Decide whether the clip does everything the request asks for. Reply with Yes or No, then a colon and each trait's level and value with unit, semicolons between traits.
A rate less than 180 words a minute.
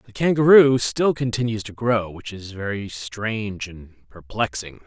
Yes: average, 150 wpm